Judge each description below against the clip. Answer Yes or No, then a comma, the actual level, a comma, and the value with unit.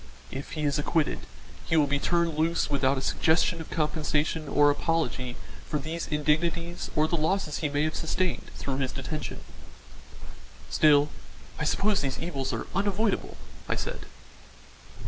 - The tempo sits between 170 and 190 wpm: No, average, 150 wpm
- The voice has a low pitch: No, medium, 155 Hz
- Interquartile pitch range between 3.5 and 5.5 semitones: No, average, 2.7 semitones